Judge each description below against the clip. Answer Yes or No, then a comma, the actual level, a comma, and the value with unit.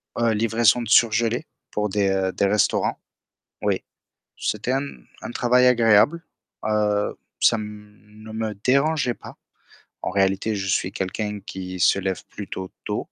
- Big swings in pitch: No, average, 2.9 semitones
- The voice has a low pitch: Yes, low, 105 Hz